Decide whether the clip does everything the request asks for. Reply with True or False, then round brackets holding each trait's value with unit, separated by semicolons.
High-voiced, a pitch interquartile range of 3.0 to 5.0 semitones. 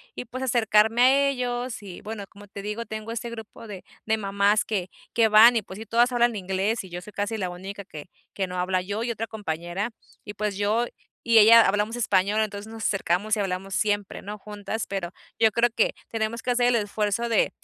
False (210 Hz; 2.6 semitones)